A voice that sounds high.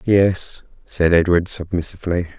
No: very low, 90 Hz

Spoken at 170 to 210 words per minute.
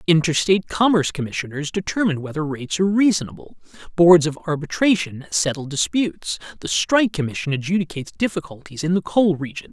No: slow, 135 wpm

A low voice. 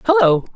No: medium, 185 Hz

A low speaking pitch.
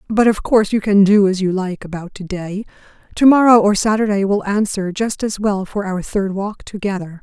No: high, 200 Hz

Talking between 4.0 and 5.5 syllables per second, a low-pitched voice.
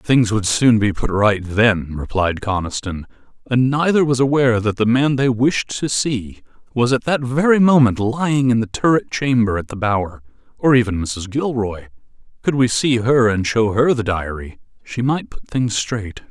Yes: 4.6 syllables/s; low, 115 Hz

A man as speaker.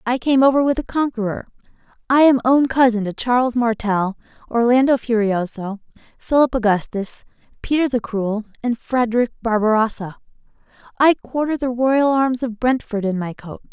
No: female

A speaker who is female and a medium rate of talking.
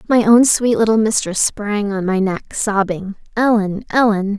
Yes: female; average, 165 wpm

